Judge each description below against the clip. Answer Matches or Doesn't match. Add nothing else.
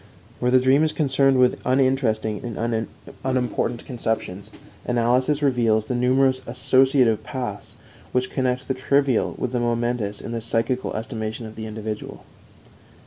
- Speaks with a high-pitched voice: Doesn't match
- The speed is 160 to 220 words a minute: Doesn't match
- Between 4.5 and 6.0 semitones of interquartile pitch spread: Doesn't match